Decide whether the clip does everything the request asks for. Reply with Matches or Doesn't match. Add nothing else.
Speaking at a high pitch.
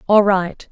Matches